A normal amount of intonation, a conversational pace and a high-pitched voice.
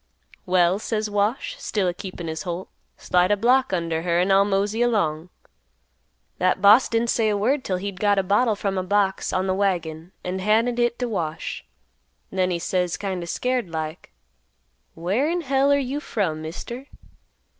Yes: average, 4.3 semitones; average, 180 wpm; high, 195 Hz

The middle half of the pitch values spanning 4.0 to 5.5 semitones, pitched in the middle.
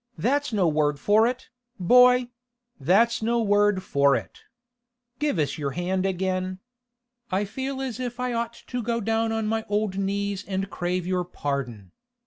No: average, 4.4 semitones; high, 200 Hz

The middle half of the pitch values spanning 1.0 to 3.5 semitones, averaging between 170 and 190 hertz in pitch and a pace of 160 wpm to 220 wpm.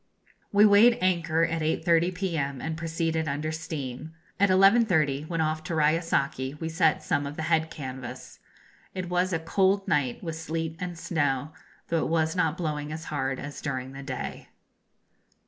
No: average, 2.7 semitones; medium, 160 Hz; average, 165 wpm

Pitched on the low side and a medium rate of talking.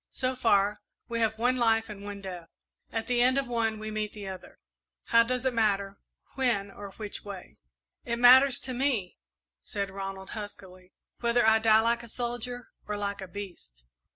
No: high, 220 Hz; average, 180 wpm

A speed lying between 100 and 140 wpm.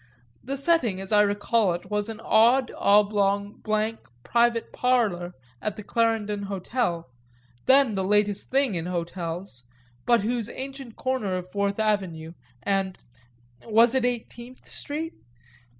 Yes: slow, 135 wpm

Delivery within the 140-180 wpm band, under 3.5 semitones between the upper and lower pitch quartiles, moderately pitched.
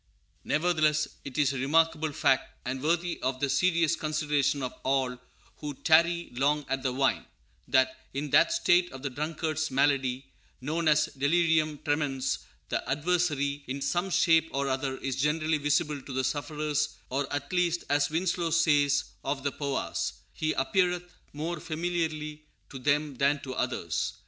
Yes: average, 155 wpm; average, 2.9 semitones; medium, 150 Hz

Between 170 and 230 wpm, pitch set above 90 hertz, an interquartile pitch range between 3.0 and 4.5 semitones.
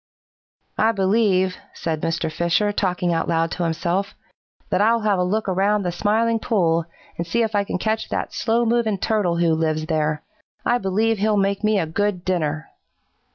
Yes: average, 180 wpm; high, 190 Hz; average, 4.2 semitones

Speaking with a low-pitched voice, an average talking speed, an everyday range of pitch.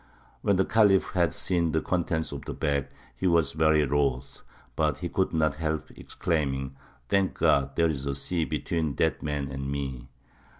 Yes: very low, 75 Hz; average, 175 wpm; average, 3.4 semitones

